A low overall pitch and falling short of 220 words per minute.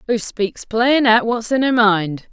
No: high, 225 Hz; fast, 205 wpm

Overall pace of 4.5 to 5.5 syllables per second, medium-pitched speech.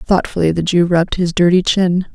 Yes: 5.3 syllables/s; medium, 175 Hz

